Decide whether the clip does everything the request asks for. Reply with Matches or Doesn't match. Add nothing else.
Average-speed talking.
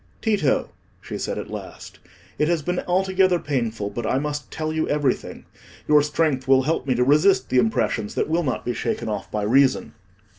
Matches